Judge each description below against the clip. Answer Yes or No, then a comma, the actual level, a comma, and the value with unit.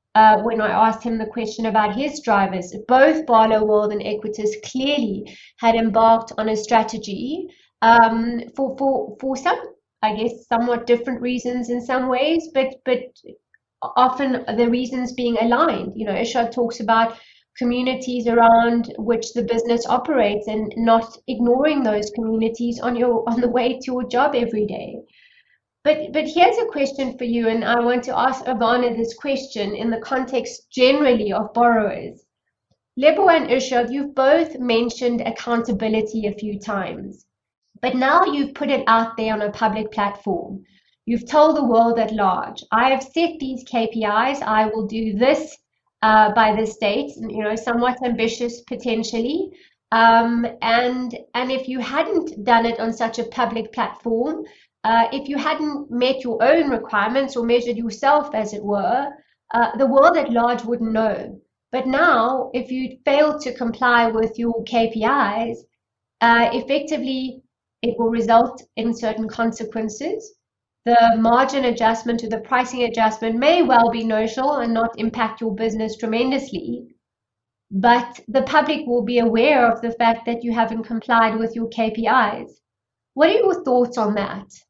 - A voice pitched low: No, high, 235 Hz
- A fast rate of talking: No, average, 160 wpm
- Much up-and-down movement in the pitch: No, narrow, 2.5 semitones